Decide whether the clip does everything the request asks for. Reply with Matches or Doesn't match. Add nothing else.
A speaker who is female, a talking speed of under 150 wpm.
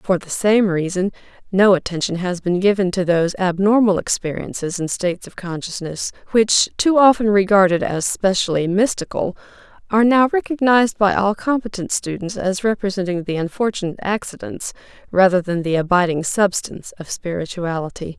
Matches